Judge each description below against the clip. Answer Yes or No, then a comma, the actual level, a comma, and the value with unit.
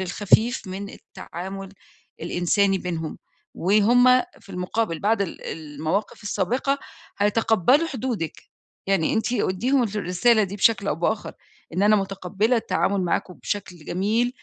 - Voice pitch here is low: No, high, 200 Hz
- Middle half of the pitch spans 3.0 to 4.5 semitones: Yes, average, 3.7 semitones